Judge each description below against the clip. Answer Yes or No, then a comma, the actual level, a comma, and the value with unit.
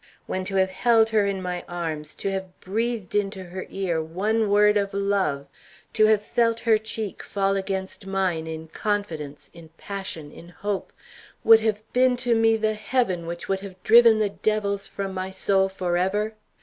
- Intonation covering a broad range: No, average, 2.9 semitones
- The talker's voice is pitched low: No, high, 195 Hz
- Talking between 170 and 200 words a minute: Yes, average, 175 wpm